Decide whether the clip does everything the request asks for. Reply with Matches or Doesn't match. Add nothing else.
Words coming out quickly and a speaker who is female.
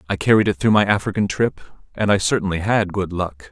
Doesn't match